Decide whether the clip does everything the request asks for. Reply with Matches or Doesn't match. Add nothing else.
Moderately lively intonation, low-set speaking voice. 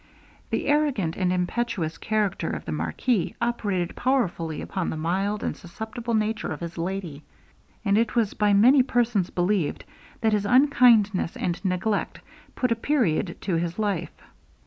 Doesn't match